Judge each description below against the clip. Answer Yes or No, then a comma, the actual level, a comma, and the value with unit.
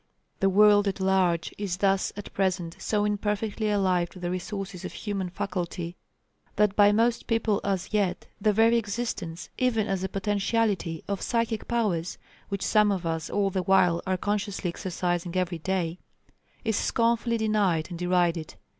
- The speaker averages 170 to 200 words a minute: No, average, 160 wpm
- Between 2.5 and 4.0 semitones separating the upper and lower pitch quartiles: Yes, average, 2.8 semitones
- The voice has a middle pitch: No, high, 195 Hz